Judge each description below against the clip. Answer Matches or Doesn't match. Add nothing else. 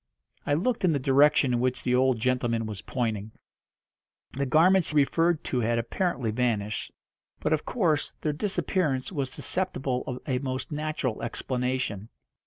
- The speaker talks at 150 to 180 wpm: Matches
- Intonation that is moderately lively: Matches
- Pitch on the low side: Matches